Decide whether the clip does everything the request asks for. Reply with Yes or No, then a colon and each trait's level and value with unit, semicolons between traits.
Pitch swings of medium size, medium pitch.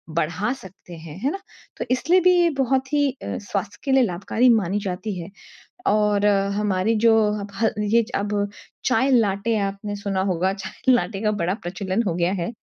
No: average, 3.6 semitones; high, 205 Hz